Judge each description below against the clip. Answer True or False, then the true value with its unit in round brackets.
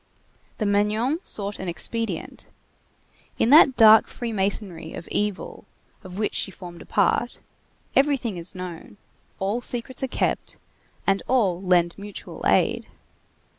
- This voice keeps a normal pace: False (130 wpm)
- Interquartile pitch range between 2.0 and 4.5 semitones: True (4.1 semitones)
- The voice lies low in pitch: False (205 Hz)